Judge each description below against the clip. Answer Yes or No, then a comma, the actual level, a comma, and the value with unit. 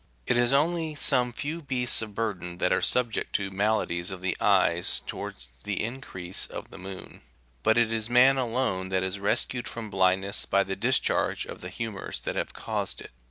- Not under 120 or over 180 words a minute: No, average, 190 wpm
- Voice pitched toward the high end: No, low, 110 Hz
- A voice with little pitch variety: No, average, 4.7 semitones